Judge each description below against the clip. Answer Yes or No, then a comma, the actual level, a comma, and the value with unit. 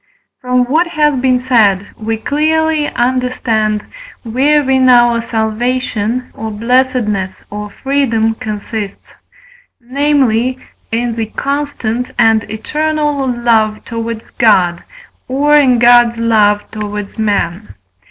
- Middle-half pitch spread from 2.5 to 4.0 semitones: Yes, average, 3.2 semitones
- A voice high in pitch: Yes, high, 235 Hz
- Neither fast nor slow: No, slow, 105 wpm